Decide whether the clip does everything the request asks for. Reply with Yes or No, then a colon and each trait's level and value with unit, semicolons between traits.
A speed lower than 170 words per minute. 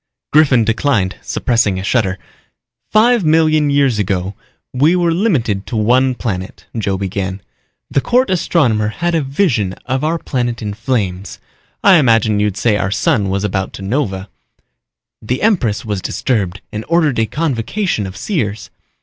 Yes: average, 150 wpm